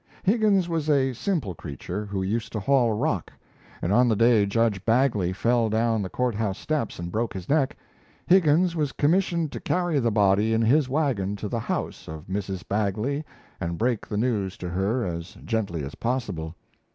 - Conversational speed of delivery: Yes, average, 185 wpm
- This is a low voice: Yes, low, 115 Hz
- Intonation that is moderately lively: No, wide, 5.8 semitones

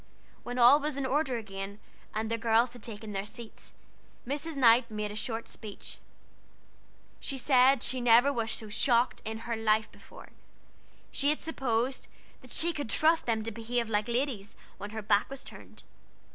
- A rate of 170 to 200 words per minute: Yes, average, 175 wpm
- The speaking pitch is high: Yes, high, 235 Hz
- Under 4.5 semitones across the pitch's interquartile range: Yes, average, 3.4 semitones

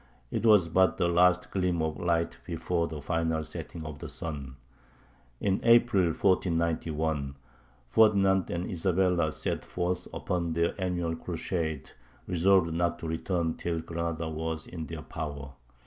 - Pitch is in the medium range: No, very low, 85 Hz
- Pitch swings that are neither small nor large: No, narrow, 2.0 semitones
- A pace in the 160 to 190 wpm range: No, average, 140 wpm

